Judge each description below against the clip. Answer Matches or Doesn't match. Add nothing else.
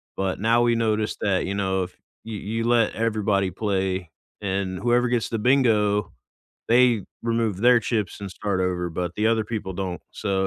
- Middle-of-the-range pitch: Doesn't match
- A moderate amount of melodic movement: Matches